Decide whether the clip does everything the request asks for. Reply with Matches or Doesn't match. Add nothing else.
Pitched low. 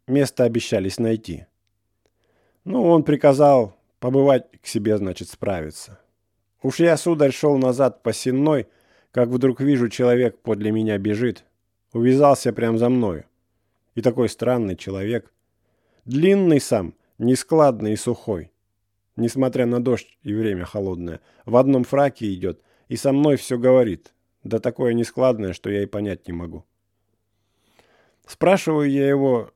Matches